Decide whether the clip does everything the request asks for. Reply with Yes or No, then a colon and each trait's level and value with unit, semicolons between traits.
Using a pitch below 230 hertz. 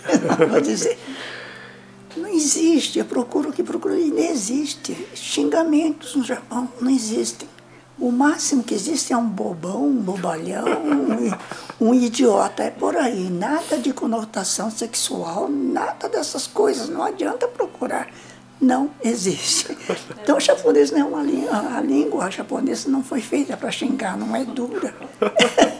No: very high, 280 Hz